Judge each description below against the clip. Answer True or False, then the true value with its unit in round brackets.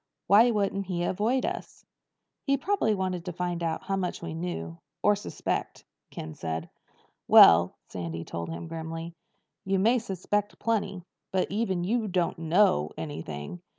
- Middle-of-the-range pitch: True (180 Hz)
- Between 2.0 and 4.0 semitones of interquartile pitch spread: False (4.5 semitones)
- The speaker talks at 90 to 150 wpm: True (145 wpm)